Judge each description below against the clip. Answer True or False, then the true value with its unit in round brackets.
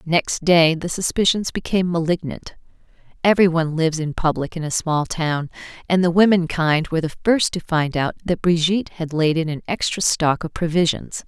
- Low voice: False (165 Hz)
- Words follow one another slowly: False (180 wpm)